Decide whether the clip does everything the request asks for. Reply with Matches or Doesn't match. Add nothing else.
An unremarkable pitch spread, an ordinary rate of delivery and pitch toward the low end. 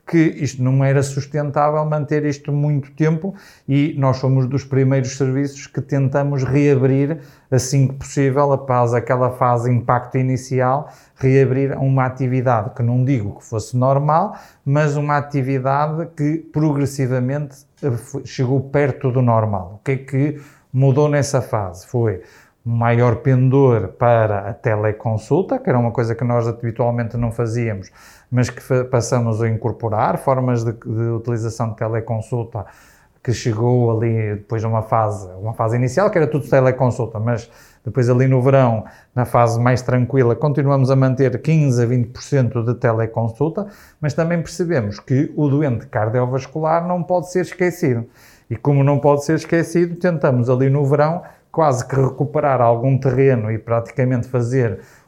Matches